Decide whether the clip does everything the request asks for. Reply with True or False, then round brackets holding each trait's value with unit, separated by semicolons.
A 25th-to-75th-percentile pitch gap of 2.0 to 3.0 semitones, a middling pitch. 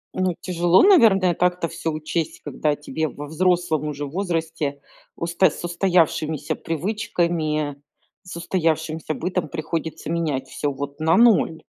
True (2.6 semitones; 165 Hz)